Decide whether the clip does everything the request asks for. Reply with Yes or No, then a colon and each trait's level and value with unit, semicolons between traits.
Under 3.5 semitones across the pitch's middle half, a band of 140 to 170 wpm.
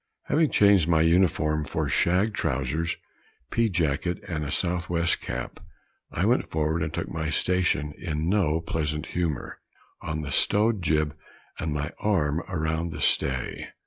Yes: average, 2.7 semitones; average, 150 wpm